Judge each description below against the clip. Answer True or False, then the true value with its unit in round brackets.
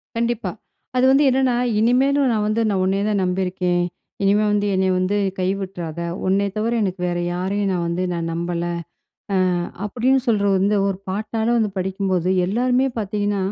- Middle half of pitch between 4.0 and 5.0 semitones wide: False (3.3 semitones)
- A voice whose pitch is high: True (200 Hz)